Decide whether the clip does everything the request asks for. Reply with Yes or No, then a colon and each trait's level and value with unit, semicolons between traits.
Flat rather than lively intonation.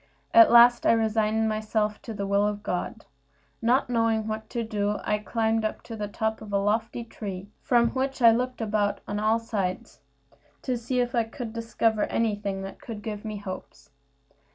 Yes: narrow, 1.8 semitones